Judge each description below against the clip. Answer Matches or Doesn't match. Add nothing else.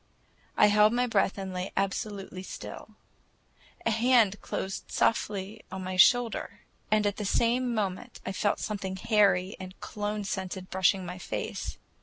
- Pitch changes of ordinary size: Doesn't match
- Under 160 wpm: Matches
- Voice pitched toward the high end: Matches